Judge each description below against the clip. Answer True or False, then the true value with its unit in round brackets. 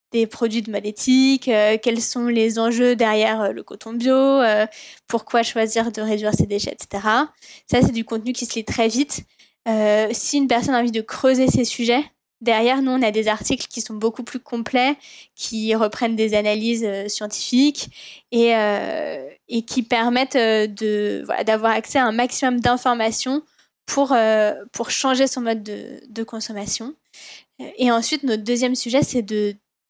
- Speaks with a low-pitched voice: False (230 Hz)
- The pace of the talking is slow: False (180 wpm)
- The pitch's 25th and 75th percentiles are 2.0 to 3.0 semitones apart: True (2.6 semitones)